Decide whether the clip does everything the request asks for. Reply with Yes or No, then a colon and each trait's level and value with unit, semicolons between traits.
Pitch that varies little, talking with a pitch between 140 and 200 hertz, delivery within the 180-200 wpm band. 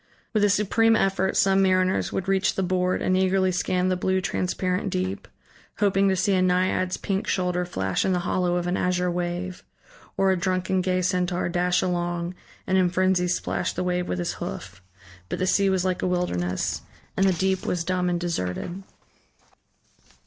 Yes: narrow, 1.0 semitones; medium, 185 Hz; average, 185 wpm